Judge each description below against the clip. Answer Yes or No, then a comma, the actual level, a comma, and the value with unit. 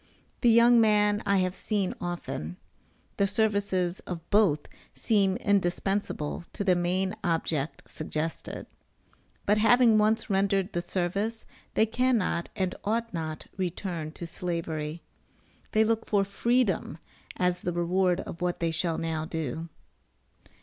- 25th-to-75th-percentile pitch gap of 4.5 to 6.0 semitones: No, average, 3.7 semitones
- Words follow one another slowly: Yes, slow, 130 wpm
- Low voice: No, medium, 185 Hz